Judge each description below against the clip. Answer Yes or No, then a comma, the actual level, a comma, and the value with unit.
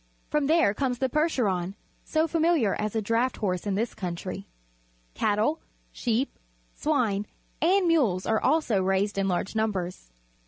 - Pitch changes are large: Yes, wide, 7.2 semitones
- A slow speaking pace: No, average, 145 wpm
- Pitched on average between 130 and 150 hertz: No, high, 220 Hz